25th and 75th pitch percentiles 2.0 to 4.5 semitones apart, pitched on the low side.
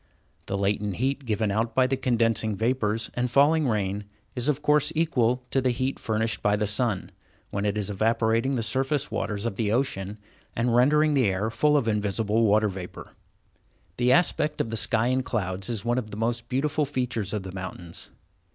Yes: average, 3.8 semitones; low, 115 Hz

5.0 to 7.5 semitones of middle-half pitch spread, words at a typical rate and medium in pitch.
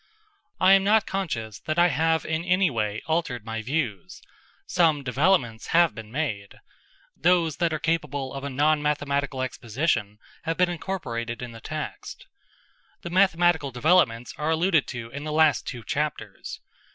Yes: wide, 5.6 semitones; average, 155 wpm; medium, 150 Hz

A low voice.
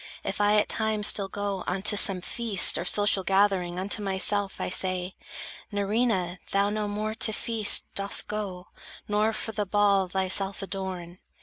No: high, 200 Hz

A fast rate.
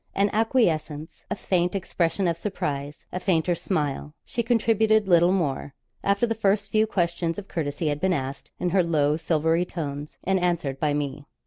No: average, 175 wpm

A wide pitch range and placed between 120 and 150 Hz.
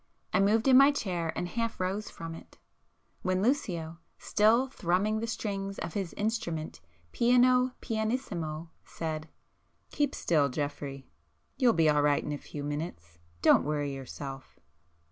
No: wide, 6.6 semitones; medium, 180 Hz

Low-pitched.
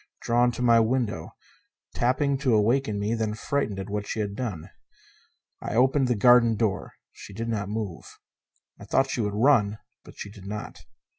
Yes: low, 110 Hz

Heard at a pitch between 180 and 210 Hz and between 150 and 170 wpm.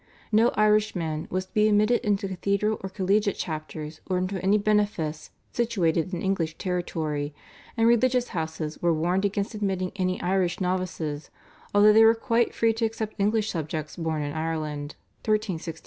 Yes: medium, 185 Hz; average, 160 wpm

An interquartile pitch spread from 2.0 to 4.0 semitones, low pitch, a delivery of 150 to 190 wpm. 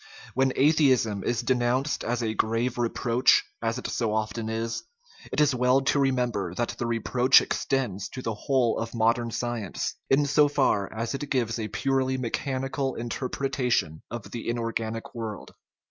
Yes: average, 2.7 semitones; low, 120 Hz; average, 165 wpm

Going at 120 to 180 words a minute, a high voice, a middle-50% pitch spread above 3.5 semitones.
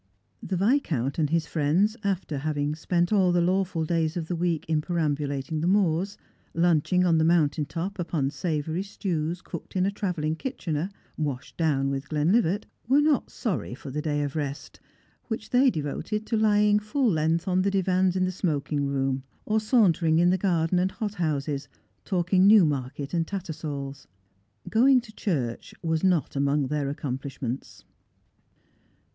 No: average, 165 wpm; medium, 165 Hz; average, 4.5 semitones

